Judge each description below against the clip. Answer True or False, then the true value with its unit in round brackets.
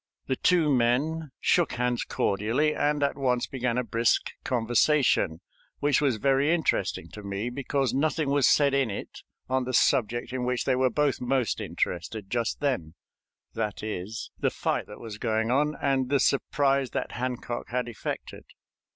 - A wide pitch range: False (3.2 semitones)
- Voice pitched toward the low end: True (125 Hz)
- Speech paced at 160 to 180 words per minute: True (165 wpm)